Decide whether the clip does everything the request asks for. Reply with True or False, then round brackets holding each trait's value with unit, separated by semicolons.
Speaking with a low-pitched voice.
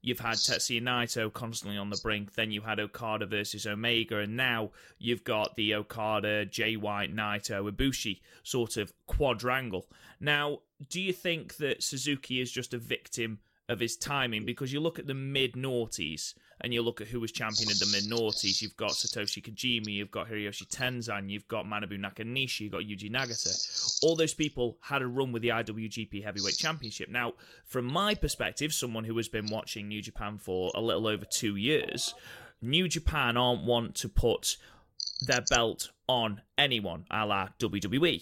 True (115 Hz)